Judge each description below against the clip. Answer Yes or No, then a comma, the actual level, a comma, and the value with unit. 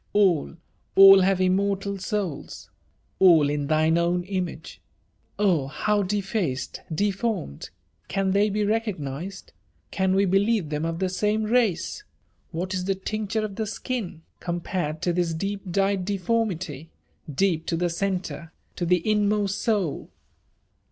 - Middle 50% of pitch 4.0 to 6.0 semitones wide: No, average, 3.3 semitones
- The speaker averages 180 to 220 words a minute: No, average, 160 wpm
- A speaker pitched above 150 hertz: Yes, high, 190 Hz